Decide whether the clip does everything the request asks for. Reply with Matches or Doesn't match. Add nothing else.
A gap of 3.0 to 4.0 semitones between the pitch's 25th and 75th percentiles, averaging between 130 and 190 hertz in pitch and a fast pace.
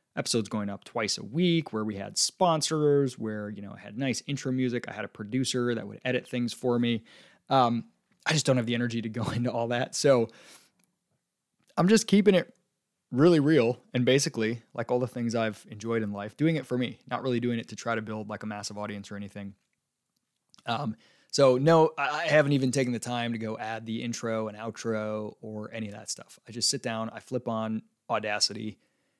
Doesn't match